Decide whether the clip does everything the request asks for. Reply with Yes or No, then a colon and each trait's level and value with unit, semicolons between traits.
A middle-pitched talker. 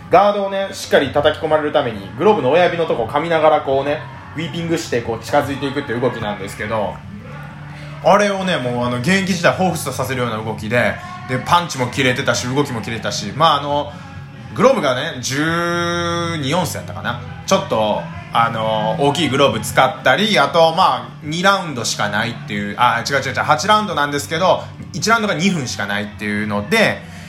Yes: medium, 145 Hz